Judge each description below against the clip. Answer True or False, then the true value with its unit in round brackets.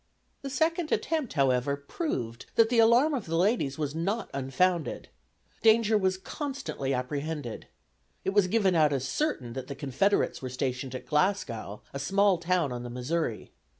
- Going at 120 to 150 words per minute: False (160 wpm)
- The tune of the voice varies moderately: False (8.3 semitones)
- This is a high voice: False (160 Hz)